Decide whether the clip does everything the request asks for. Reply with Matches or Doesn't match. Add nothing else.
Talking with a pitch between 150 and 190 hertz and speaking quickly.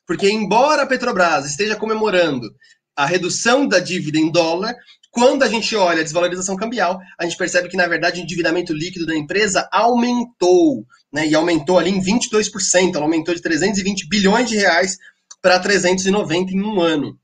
Doesn't match